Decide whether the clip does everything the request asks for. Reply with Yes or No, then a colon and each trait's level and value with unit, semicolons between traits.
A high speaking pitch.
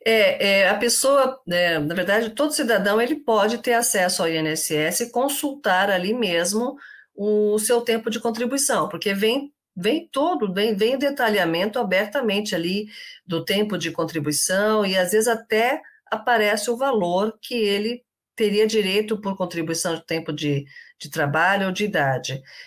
Yes: high, 210 Hz